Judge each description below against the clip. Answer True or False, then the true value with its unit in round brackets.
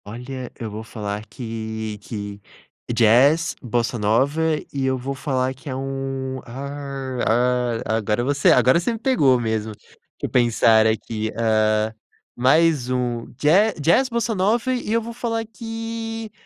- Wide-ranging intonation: True (6.0 semitones)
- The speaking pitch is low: True (130 Hz)